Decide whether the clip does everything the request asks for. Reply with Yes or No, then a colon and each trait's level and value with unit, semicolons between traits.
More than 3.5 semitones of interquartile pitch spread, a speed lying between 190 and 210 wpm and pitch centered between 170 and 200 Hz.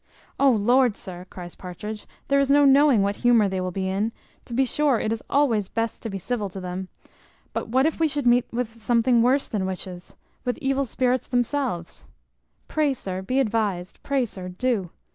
No: wide, 5.5 semitones; average, 195 wpm; high, 230 Hz